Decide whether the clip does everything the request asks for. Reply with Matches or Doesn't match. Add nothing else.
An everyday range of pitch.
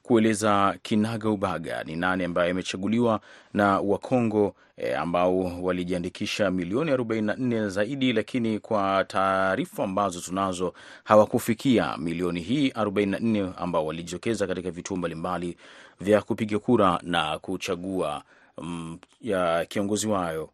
Matches